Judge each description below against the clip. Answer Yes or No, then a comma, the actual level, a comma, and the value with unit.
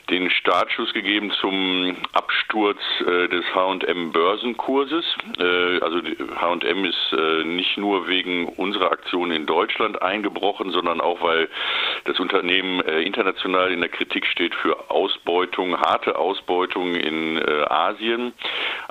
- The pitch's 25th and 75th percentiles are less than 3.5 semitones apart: Yes, narrow, 2.5 semitones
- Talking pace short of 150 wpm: Yes, average, 130 wpm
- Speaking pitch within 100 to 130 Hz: No, very low, 90 Hz